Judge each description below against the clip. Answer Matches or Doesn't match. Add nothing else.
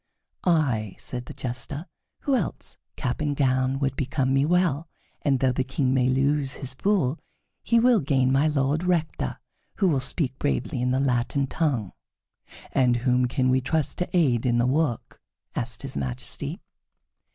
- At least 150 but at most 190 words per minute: Matches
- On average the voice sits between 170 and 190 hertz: Doesn't match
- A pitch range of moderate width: Matches